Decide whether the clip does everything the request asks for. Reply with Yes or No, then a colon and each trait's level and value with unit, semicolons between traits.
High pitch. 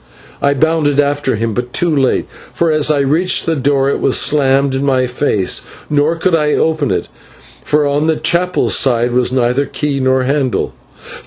No: medium, 140 Hz